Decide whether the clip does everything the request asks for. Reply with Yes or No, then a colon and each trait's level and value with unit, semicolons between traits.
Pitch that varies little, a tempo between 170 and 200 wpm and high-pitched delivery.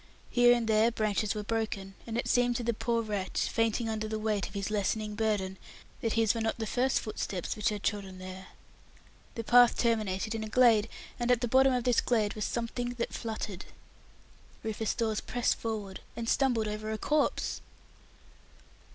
Yes: narrow, 2.0 semitones; average, 185 wpm; high, 220 Hz